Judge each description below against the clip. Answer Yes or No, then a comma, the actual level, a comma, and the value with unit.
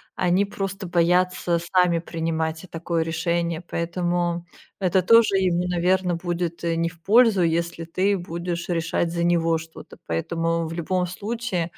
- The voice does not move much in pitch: Yes, narrow, 1.6 semitones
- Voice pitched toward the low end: No, medium, 175 Hz